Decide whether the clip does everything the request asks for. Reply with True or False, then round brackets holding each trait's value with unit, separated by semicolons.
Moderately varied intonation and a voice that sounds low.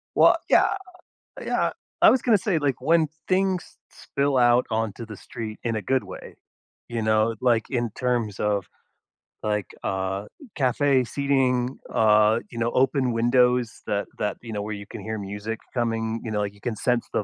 True (3.1 semitones; 115 Hz)